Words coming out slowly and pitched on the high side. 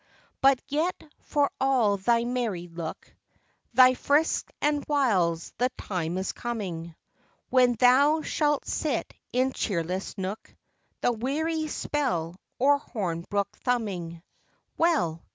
Yes: slow, 115 wpm; high, 240 Hz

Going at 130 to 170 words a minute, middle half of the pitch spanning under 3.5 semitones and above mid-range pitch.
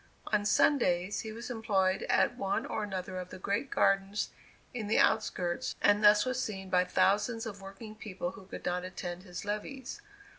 No: average, 180 wpm; average, 2.7 semitones; high, 200 Hz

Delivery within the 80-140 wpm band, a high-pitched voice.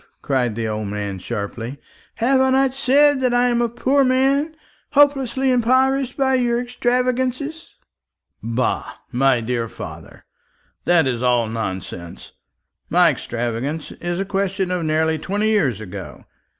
Yes: slow, 135 wpm; high, 195 Hz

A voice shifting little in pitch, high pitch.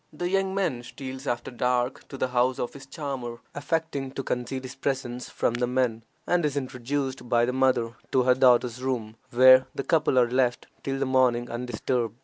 No: narrow, 1.9 semitones; low, 130 Hz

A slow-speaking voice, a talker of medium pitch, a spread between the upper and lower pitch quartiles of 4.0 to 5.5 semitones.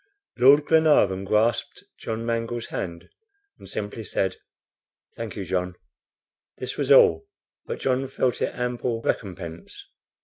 No: slow, 125 wpm; low, 115 Hz; average, 4.5 semitones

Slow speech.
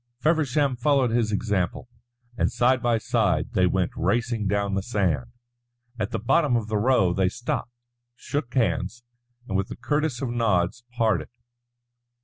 No: average, 150 wpm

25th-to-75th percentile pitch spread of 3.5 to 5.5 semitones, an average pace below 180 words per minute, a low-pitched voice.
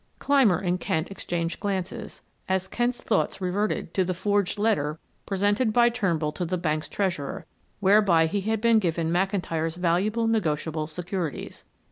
No: average, 3.8 semitones; average, 145 wpm; medium, 185 Hz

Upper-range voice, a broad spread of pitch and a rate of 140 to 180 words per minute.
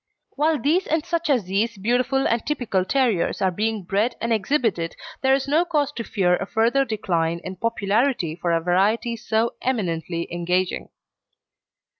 Yes: high, 225 Hz; wide, 6.3 semitones; average, 160 wpm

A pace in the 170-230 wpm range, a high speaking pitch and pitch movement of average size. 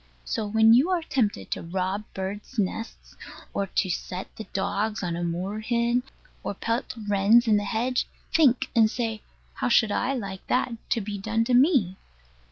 Yes: average, 175 wpm; high, 220 Hz; average, 3.4 semitones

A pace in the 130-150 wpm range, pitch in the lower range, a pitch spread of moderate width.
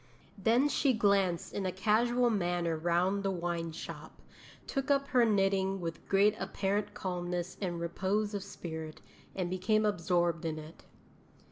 No: average, 145 wpm; high, 190 Hz; average, 3.3 semitones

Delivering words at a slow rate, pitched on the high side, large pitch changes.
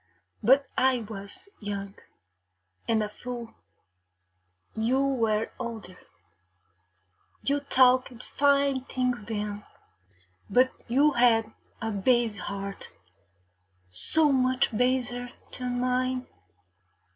No: slow, 90 wpm; high, 245 Hz; average, 2.9 semitones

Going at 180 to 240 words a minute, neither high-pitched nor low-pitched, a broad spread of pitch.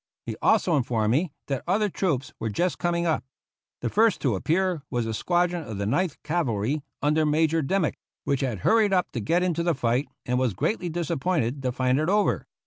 Yes: average, 200 wpm; medium, 155 Hz; wide, 5.9 semitones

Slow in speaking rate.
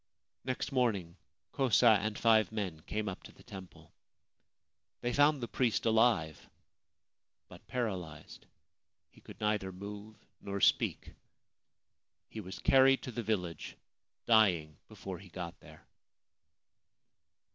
Yes: slow, 120 wpm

